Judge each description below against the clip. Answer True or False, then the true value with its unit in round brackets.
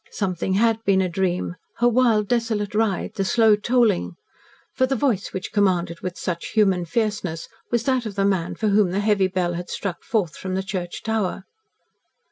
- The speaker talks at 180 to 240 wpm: True (185 wpm)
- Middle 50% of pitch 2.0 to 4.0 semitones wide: True (3.4 semitones)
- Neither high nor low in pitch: False (200 Hz)